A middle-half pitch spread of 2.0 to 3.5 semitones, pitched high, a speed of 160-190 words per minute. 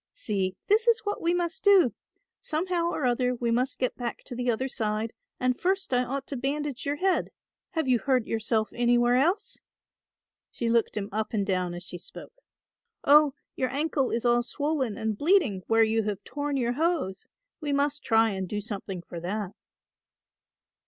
No: average, 5.2 semitones; very high, 250 Hz; average, 180 wpm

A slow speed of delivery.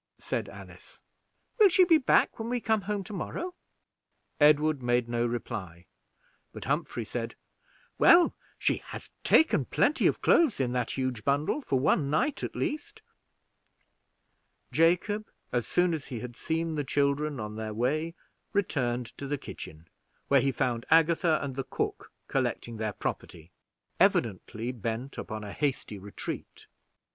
No: average, 150 wpm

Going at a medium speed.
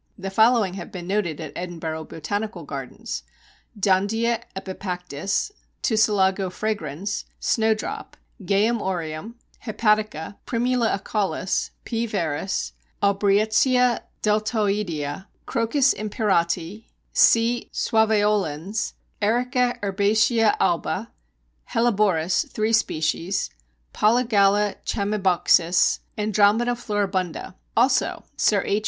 No: slow, 85 wpm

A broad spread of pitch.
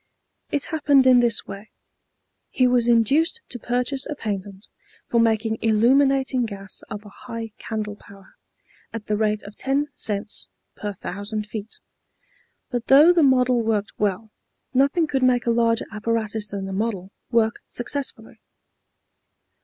No: average, 3.4 semitones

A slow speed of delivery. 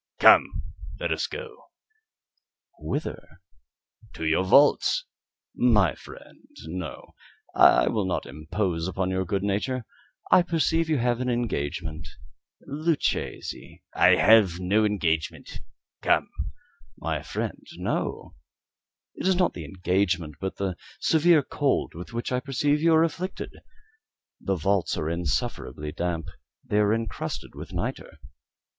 Yes: slow, 125 wpm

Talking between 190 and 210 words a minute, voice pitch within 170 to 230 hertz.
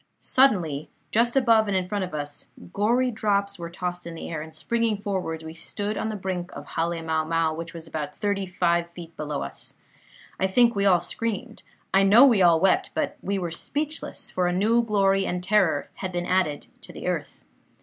Yes: fast, 205 wpm; medium, 185 Hz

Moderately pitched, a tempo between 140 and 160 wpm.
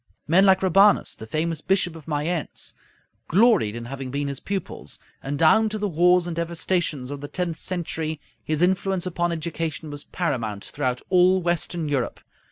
No: medium, 165 Hz; average, 170 wpm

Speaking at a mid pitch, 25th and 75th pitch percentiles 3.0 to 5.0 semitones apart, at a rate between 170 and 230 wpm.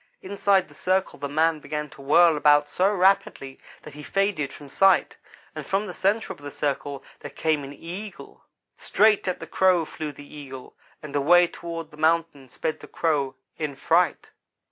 Yes: medium, 160 Hz; average, 4.3 semitones; average, 180 wpm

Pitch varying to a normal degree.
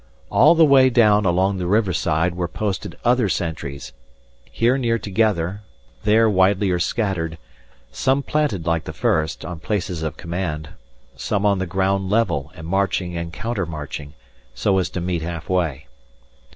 Yes: average, 4.1 semitones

